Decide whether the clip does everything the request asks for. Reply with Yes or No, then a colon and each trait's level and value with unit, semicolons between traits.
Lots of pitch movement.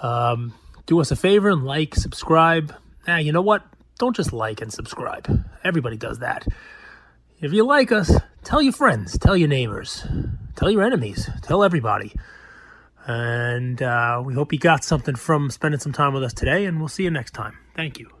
Yes: wide, 6.2 semitones